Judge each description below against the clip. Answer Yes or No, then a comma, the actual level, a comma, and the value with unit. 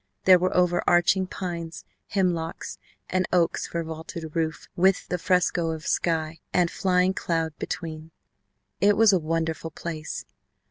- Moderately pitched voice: Yes, medium, 170 Hz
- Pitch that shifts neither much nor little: No, narrow, 2.0 semitones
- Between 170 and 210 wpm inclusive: No, average, 140 wpm